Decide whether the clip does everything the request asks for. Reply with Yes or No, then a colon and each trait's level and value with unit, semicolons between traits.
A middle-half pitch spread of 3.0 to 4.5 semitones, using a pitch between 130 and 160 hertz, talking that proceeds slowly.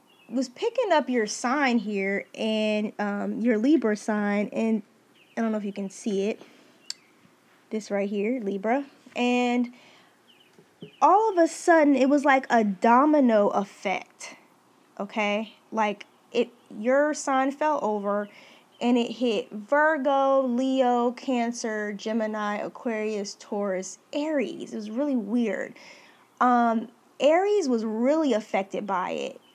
No: average, 4.2 semitones; high, 235 Hz; slow, 130 wpm